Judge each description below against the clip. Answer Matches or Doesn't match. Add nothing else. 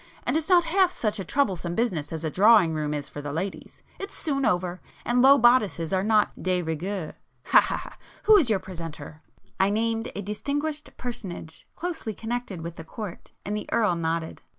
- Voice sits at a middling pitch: Doesn't match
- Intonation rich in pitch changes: Matches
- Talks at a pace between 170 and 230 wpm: Matches